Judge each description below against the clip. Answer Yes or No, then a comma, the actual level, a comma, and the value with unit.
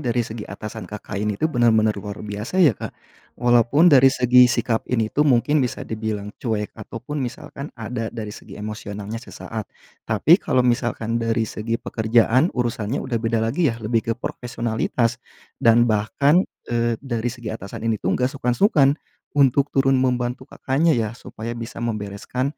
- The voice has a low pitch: Yes, low, 115 Hz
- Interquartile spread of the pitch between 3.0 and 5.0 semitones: No, narrow, 2.6 semitones